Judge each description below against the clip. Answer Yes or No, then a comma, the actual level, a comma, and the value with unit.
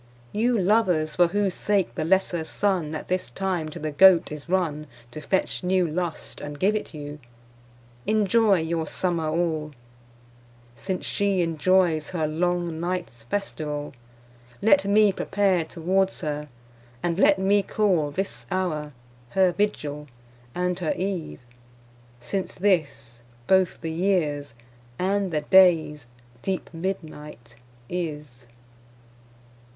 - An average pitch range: Yes, average, 3.8 semitones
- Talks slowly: Yes, slow, 125 wpm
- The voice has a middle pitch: Yes, medium, 175 Hz